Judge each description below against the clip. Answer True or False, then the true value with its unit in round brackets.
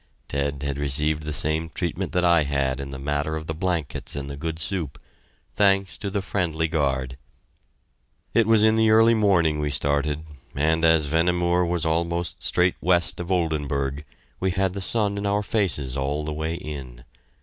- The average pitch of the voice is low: True (80 Hz)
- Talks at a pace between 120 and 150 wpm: False (180 wpm)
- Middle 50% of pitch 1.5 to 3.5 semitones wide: False (4.1 semitones)